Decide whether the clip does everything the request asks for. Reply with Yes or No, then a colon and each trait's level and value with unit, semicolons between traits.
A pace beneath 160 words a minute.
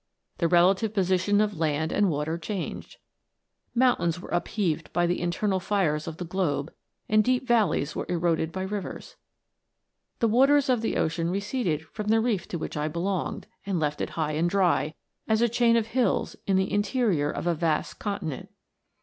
No: average, 175 wpm